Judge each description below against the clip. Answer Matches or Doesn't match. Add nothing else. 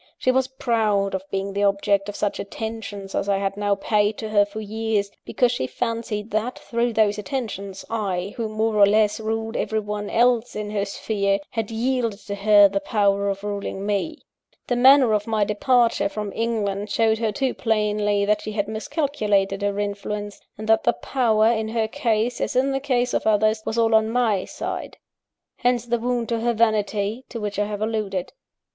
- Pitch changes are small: Matches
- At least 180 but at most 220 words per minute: Matches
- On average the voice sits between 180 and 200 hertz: Doesn't match